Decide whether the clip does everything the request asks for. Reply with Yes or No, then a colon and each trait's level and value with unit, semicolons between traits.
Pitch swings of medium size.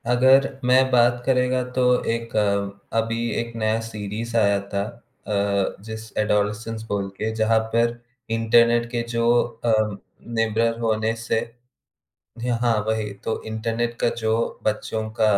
No: narrow, 1.3 semitones